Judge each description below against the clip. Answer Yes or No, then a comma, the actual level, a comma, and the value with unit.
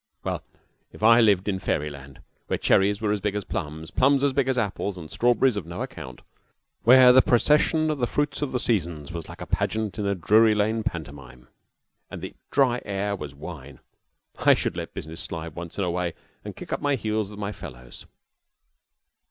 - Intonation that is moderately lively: No, wide, 6.5 semitones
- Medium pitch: No, low, 100 Hz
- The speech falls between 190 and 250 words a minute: Yes, average, 200 wpm